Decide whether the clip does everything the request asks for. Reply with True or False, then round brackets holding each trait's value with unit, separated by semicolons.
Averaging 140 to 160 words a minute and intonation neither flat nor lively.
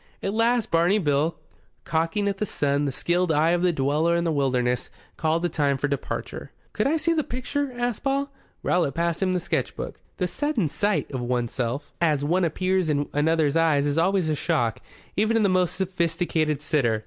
False (195 wpm; 4.7 semitones)